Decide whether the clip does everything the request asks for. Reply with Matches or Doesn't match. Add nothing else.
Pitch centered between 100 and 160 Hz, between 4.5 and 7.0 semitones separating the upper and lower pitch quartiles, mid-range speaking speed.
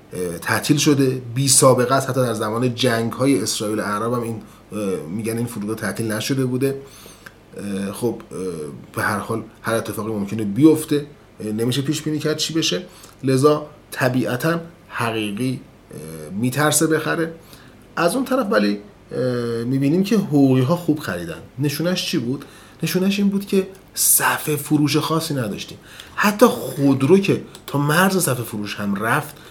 Matches